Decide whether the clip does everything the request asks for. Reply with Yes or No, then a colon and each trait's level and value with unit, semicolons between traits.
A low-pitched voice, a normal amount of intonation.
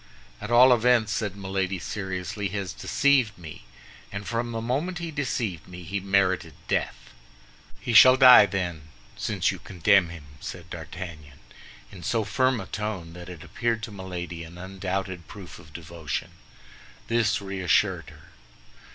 Yes: very low, 95 Hz; average, 4.3 semitones